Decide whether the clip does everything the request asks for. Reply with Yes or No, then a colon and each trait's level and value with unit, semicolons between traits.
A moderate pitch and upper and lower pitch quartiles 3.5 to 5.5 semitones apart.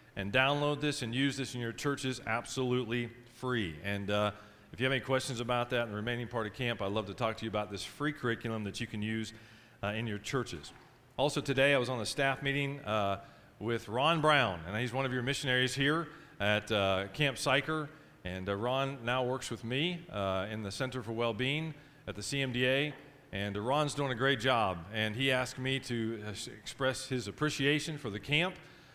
No: low, 125 Hz; average, 4.2 semitones